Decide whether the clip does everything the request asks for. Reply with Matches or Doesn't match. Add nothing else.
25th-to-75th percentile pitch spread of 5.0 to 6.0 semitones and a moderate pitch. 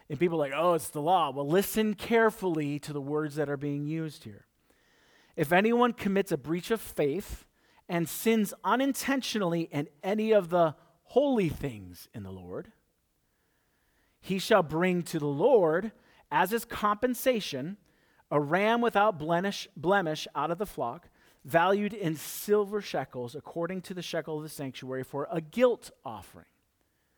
Matches